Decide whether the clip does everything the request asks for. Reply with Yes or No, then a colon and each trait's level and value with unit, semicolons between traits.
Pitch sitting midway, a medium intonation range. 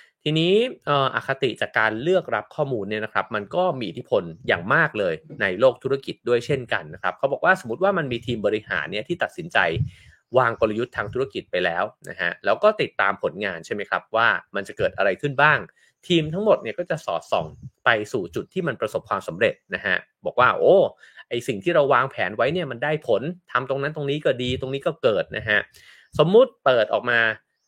No: medium, 150 Hz; wide, 7.9 semitones